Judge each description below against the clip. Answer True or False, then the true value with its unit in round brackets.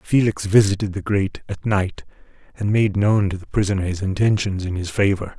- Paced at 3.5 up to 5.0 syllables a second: False (5.5 syllables/s)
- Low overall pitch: True (100 Hz)